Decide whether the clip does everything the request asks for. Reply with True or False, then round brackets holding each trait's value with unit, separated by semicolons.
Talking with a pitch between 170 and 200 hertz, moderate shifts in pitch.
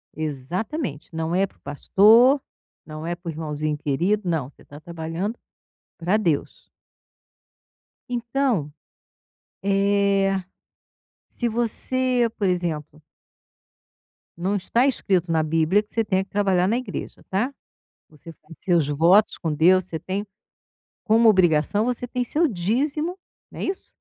False (190 Hz; 5.8 semitones)